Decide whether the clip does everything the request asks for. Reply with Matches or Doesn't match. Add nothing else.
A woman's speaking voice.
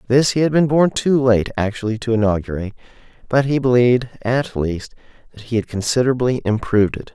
Doesn't match